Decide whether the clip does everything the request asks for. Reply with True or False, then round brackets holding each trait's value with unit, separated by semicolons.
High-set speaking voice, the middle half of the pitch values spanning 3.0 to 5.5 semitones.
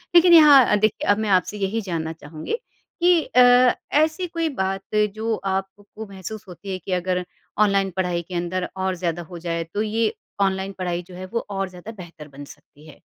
True (195 Hz; 3.6 semitones)